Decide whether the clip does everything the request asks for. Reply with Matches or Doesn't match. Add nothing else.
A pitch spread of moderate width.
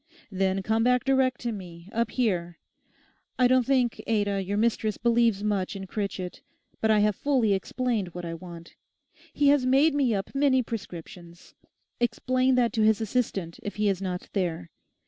Matches